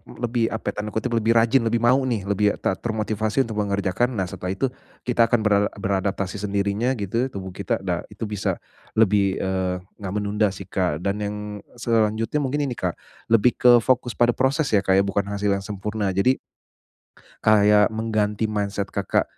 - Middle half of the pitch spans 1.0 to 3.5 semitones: Yes, narrow, 2.6 semitones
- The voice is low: Yes, low, 105 Hz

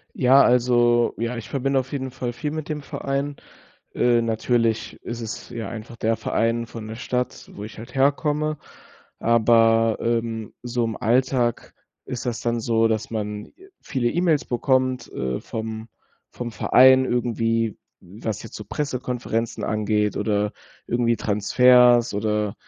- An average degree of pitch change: No, narrow, 2.2 semitones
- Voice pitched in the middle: No, low, 120 Hz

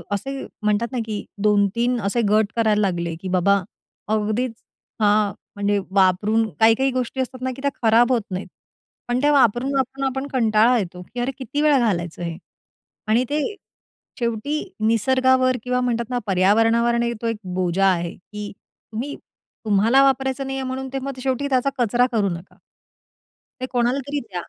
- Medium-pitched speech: No, high, 235 Hz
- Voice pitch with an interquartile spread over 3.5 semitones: Yes, average, 4.0 semitones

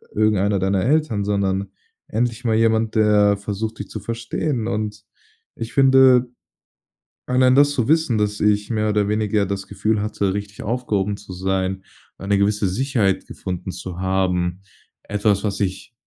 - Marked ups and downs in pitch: No, narrow, 2.5 semitones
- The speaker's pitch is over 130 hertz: No, low, 105 Hz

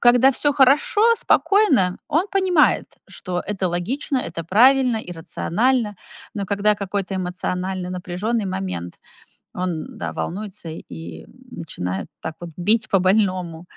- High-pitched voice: Yes, high, 195 Hz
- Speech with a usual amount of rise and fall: No, wide, 5.9 semitones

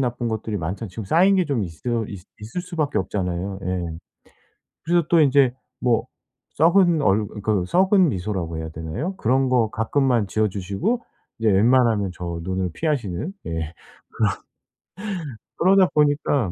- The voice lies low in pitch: Yes, low, 115 Hz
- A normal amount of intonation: No, wide, 7.7 semitones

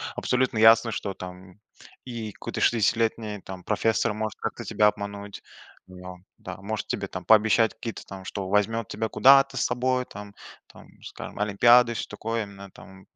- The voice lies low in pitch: Yes, low, 105 Hz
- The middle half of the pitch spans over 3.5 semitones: No, narrow, 2.6 semitones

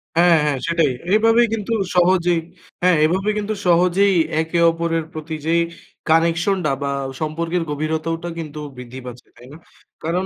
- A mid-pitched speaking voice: Yes, medium, 170 Hz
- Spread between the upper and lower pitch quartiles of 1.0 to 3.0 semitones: Yes, narrow, 2.4 semitones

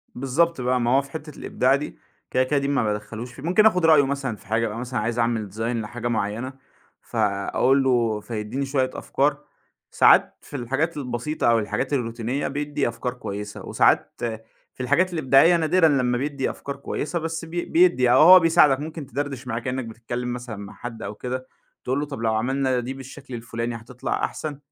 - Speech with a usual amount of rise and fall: Yes, average, 3.6 semitones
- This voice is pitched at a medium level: No, low, 130 Hz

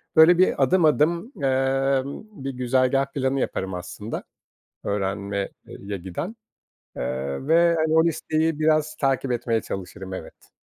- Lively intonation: Yes, wide, 7.7 semitones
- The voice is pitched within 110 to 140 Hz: Yes, low, 135 Hz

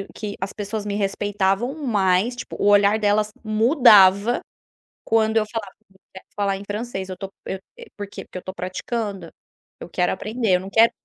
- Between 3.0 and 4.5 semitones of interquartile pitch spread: No, narrow, 2.4 semitones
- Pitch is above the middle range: Yes, high, 205 Hz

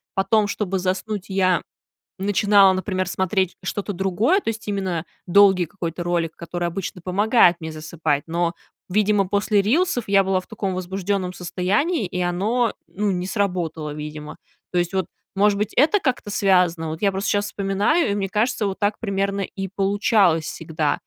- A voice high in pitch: Yes, high, 195 Hz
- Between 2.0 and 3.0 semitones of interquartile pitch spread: Yes, narrow, 2.6 semitones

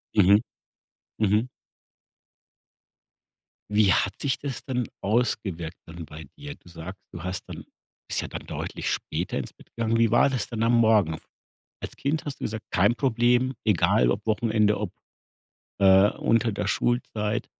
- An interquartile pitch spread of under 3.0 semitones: No, average, 3.7 semitones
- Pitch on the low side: Yes, low, 110 Hz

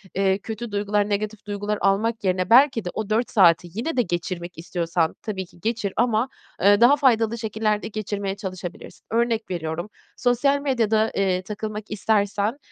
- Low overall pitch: No, high, 210 Hz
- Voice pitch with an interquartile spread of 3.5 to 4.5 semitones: No, average, 2.8 semitones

